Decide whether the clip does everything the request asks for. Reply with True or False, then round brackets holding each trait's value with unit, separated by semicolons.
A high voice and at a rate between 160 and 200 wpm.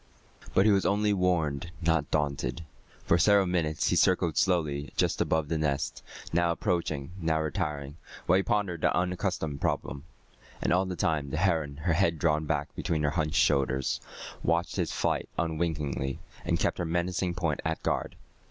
False (80 Hz; 170 wpm)